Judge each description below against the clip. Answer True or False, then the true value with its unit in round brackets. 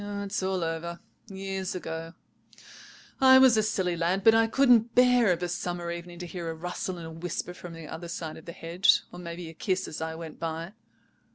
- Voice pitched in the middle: True (175 Hz)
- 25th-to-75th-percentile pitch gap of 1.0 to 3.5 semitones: True (2.9 semitones)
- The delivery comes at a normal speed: False (210 wpm)